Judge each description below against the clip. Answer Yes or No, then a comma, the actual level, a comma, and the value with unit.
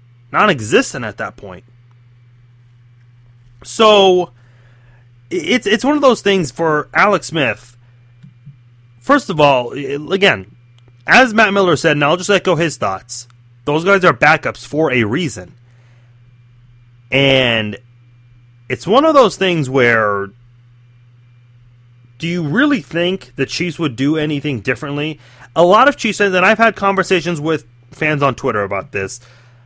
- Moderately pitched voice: No, low, 125 Hz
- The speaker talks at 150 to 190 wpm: No, average, 140 wpm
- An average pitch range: No, wide, 6.1 semitones